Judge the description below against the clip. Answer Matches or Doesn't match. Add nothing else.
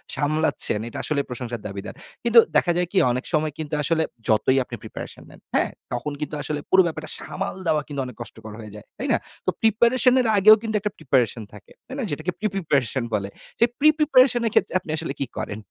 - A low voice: Doesn't match